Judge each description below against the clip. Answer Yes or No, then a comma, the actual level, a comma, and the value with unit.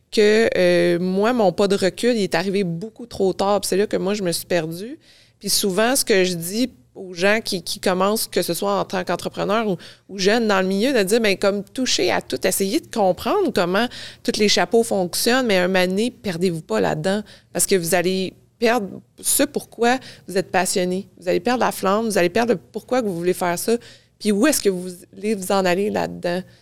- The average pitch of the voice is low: No, high, 200 Hz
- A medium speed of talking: No, fast, 225 wpm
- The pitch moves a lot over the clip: No, average, 3.3 semitones